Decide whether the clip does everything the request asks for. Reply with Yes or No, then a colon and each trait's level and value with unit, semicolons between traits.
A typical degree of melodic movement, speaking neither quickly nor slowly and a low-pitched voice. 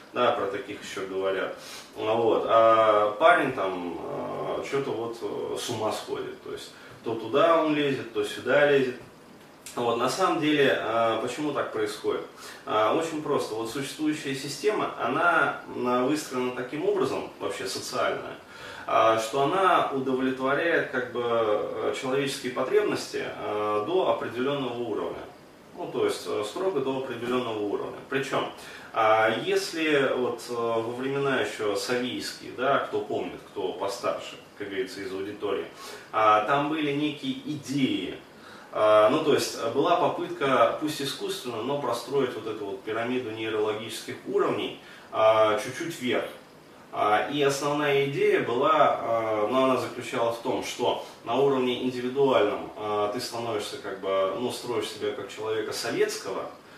No: wide, 6.4 semitones; average, 125 wpm; low, 130 Hz